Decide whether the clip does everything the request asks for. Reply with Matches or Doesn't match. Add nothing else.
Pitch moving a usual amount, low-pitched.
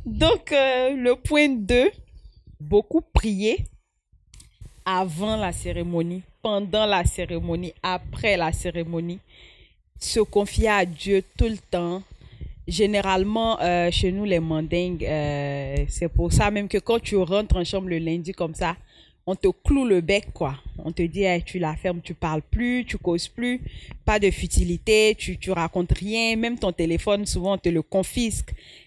Doesn't match